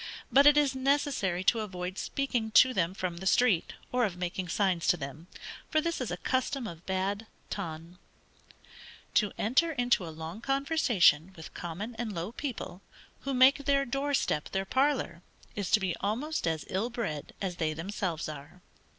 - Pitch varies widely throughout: Yes, wide, 6.9 semitones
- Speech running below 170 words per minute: No, average, 175 wpm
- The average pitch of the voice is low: No, high, 200 Hz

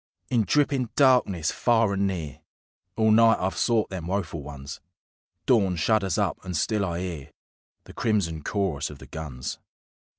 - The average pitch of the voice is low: Yes, very low, 95 Hz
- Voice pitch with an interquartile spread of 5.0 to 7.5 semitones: Yes, wide, 5.6 semitones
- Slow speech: No, average, 155 wpm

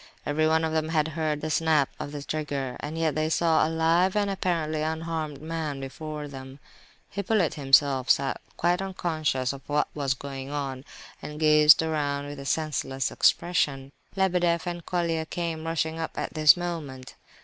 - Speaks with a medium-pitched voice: Yes, medium, 155 Hz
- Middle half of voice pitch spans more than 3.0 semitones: No, narrow, 2.4 semitones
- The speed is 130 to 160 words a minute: No, average, 170 wpm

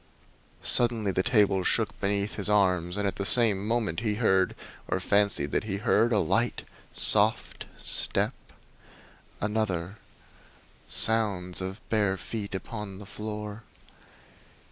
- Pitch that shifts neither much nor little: No, narrow, 2.1 semitones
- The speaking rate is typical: No, slow, 130 wpm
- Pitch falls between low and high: No, low, 105 Hz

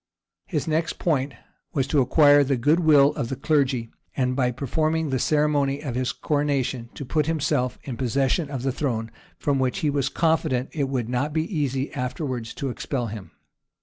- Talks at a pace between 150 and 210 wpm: Yes, average, 180 wpm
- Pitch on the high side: No, medium, 140 Hz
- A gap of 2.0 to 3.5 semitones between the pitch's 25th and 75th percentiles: Yes, average, 2.9 semitones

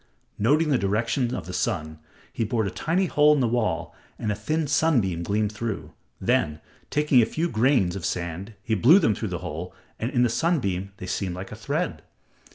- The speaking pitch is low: Yes, low, 110 Hz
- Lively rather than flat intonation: Yes, wide, 7.1 semitones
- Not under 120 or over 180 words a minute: No, average, 200 wpm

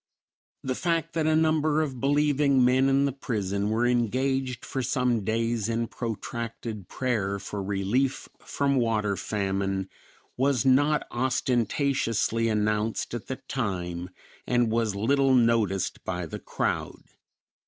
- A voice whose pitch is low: Yes, low, 120 Hz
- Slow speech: Yes, slow, 130 wpm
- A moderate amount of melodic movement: Yes, average, 4.2 semitones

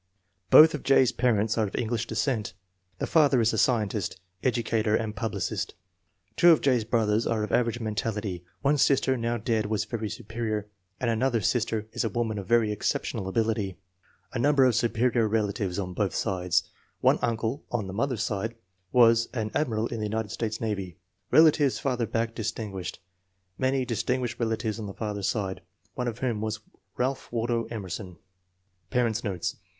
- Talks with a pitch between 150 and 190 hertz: No, low, 115 Hz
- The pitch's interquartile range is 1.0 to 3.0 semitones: Yes, narrow, 2.4 semitones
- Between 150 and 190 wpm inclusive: Yes, average, 170 wpm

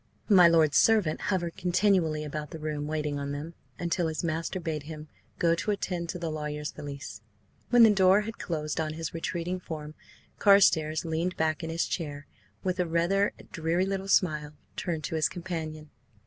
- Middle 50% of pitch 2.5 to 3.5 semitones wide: Yes, average, 2.9 semitones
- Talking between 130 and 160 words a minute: No, average, 180 wpm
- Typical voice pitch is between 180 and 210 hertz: No, medium, 165 Hz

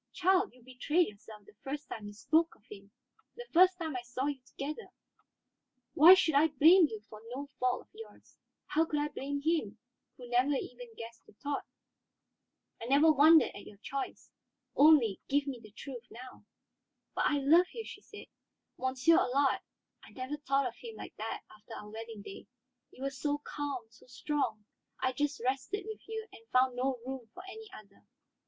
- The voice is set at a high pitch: Yes, very high, 275 Hz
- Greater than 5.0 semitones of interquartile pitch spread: No, average, 4.4 semitones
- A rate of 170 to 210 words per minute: Yes, average, 185 wpm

